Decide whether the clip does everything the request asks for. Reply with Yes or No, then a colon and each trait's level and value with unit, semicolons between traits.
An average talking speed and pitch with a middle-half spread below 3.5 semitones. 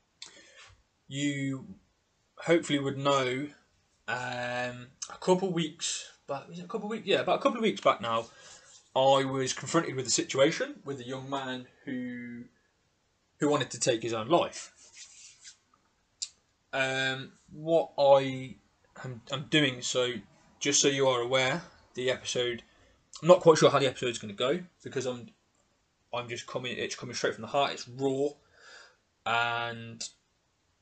Yes: average, 150 wpm; average, 3.1 semitones